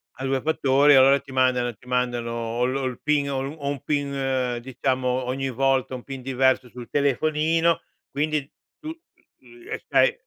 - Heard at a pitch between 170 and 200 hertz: No, low, 135 Hz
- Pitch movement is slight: Yes, narrow, 2.2 semitones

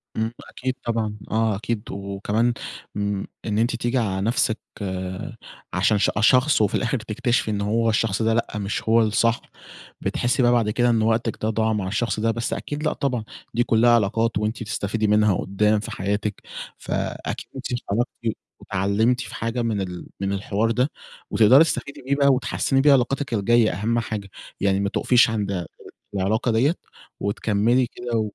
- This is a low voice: Yes, low, 110 Hz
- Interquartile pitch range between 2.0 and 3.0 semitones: Yes, narrow, 2.6 semitones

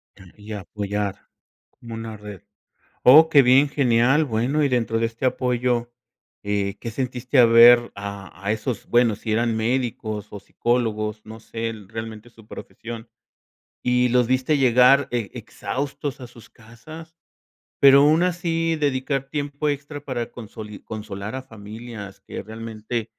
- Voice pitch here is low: Yes, low, 120 Hz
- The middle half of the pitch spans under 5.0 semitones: Yes, average, 3.3 semitones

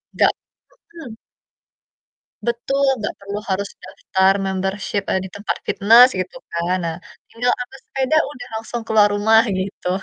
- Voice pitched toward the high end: Yes, high, 205 Hz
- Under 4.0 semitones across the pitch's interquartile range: No, average, 4.3 semitones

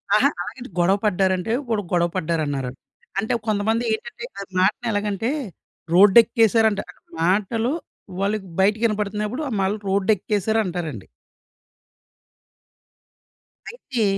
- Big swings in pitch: No, average, 2.9 semitones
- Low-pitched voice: No, high, 205 Hz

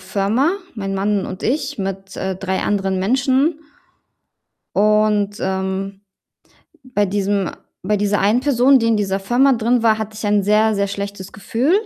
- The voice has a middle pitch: No, high, 205 Hz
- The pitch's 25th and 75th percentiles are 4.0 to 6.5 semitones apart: No, average, 2.8 semitones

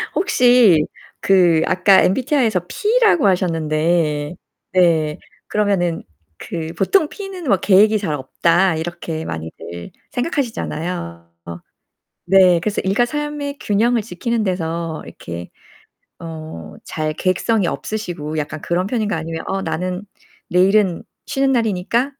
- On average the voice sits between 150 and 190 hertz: Yes, medium, 185 Hz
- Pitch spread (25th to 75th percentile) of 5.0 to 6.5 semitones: Yes, wide, 5.4 semitones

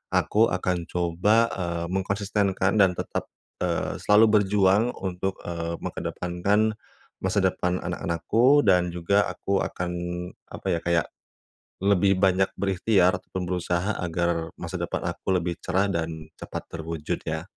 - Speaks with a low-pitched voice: Yes, very low, 90 Hz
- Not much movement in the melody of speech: Yes, narrow, 2.1 semitones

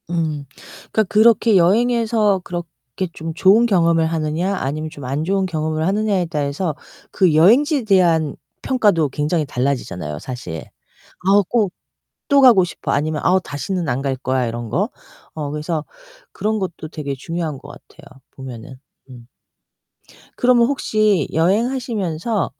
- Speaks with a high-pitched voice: No, medium, 170 Hz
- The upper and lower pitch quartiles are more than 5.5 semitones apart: Yes, wide, 5.9 semitones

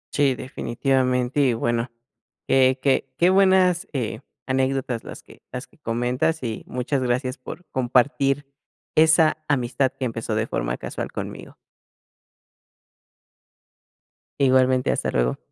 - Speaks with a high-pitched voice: No, low, 130 Hz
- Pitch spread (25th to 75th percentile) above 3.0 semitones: No, narrow, 2.5 semitones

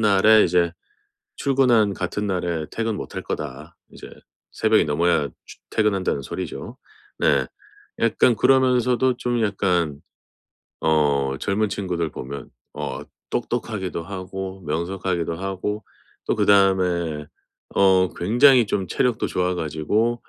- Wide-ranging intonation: No, average, 4.4 semitones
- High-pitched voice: No, very low, 95 Hz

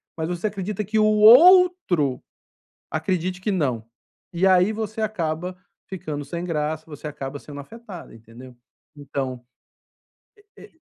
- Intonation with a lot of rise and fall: Yes, wide, 6.5 semitones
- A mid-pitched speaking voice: Yes, medium, 175 Hz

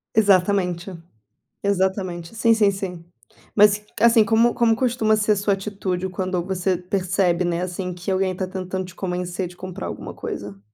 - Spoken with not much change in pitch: Yes, narrow, 2.2 semitones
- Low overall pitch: No, high, 190 Hz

